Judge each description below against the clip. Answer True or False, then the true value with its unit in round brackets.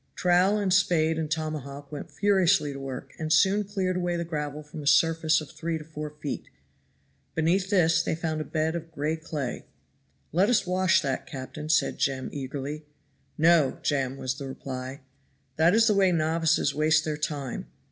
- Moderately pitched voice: True (155 Hz)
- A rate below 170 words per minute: False (180 wpm)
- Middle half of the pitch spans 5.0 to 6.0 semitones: False (3.1 semitones)